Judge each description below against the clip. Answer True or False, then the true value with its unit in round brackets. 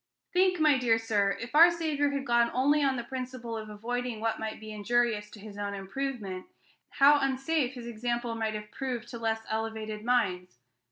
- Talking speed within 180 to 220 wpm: True (185 wpm)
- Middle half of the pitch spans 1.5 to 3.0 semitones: False (3.6 semitones)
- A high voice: True (235 Hz)